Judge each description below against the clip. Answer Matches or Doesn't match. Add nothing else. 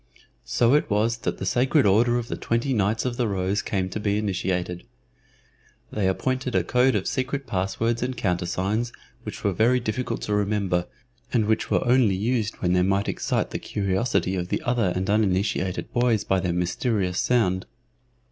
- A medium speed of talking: Matches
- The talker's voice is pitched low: Matches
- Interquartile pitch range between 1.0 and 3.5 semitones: Doesn't match